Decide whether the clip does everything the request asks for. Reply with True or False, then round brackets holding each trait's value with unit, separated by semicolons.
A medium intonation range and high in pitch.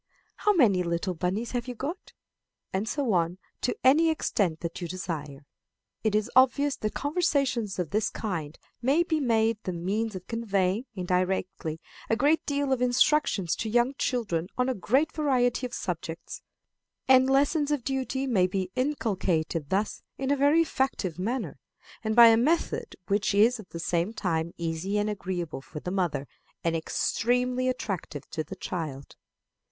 False (6.5 semitones; 215 Hz)